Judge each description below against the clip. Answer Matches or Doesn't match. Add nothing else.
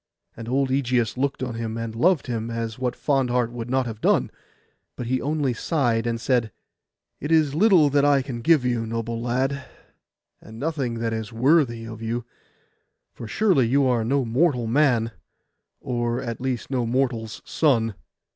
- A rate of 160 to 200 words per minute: Matches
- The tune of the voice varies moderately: Matches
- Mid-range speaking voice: Doesn't match